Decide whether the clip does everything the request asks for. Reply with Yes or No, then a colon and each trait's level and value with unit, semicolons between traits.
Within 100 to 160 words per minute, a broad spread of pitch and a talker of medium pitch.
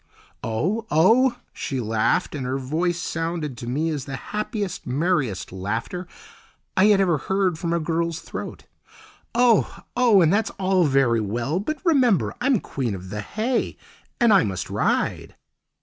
Yes: average, 150 wpm; wide, 7.9 semitones; medium, 165 Hz